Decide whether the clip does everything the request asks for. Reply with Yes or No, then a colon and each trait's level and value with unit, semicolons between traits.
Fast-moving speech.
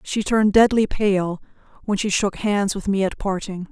No: average, 195 wpm